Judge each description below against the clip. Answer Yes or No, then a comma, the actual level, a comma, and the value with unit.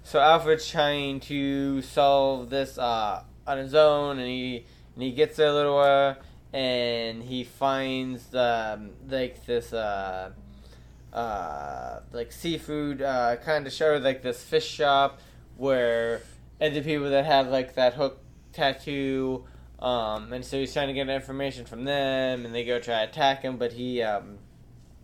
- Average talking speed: Yes, average, 165 wpm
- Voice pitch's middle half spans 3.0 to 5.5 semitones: No, narrow, 2.6 semitones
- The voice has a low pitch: Yes, low, 130 Hz